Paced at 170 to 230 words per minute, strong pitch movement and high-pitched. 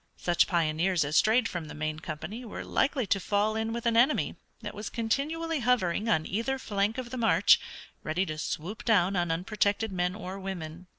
No: average, 190 wpm; average, 4.9 semitones; high, 200 Hz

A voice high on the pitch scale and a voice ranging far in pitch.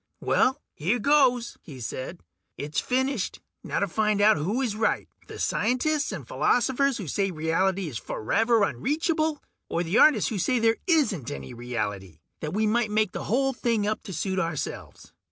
Yes: high, 215 Hz; wide, 7.5 semitones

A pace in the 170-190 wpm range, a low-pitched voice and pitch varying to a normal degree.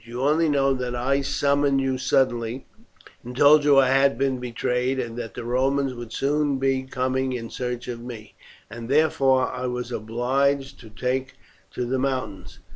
No: average, 175 wpm; low, 130 Hz; narrow, 1.9 semitones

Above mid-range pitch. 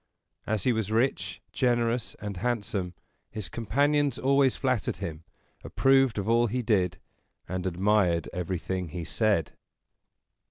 No: low, 110 Hz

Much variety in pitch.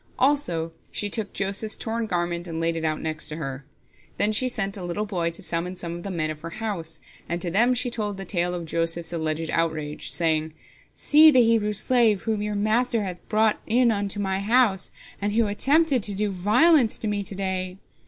No: average, 4.6 semitones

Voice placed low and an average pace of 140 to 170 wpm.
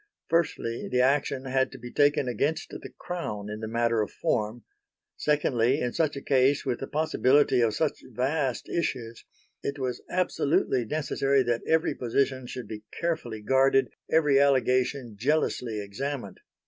Yes: low, 130 Hz; average, 150 wpm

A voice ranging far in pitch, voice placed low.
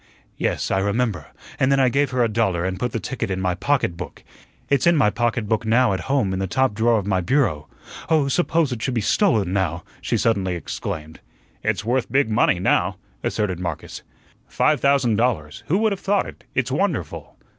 Yes: wide, 6.2 semitones; low, 115 Hz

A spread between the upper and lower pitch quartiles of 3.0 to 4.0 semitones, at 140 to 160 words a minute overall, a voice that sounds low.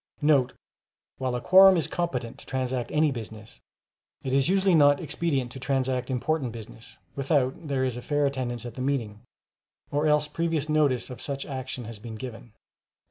No: average, 3.4 semitones; average, 175 wpm; low, 130 Hz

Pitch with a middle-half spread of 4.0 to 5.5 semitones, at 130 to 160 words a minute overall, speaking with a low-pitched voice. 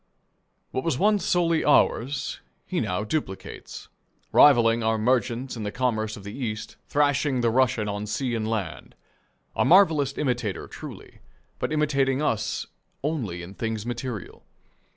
Yes: average, 4.6 semitones; average, 140 wpm; low, 120 Hz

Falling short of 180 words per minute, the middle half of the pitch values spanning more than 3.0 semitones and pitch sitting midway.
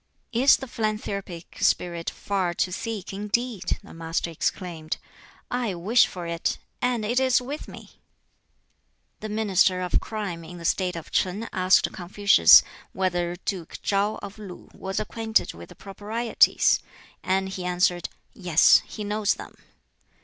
No: average, 140 wpm; average, 3.4 semitones; high, 195 Hz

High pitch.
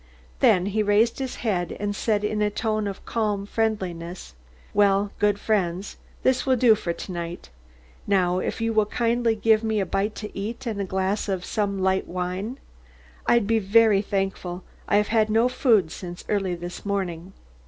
Yes: high, 205 Hz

